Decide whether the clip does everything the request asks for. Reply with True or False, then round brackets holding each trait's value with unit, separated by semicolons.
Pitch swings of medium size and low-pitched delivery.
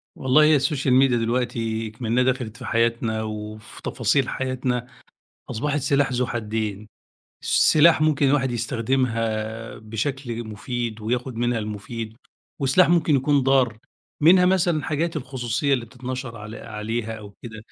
True (3.3 semitones; 120 Hz)